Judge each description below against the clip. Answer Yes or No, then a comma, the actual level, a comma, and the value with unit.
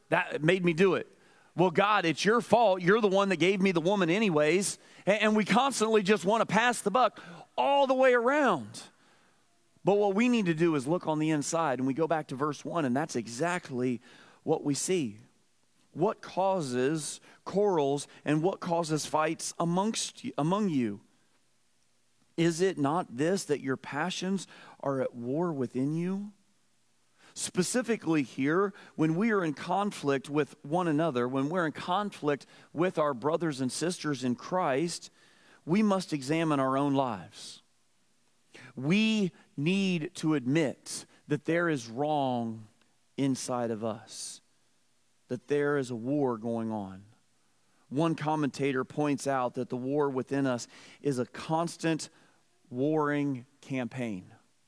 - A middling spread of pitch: No, wide, 5.8 semitones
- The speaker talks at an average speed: Yes, average, 150 wpm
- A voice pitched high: No, medium, 155 Hz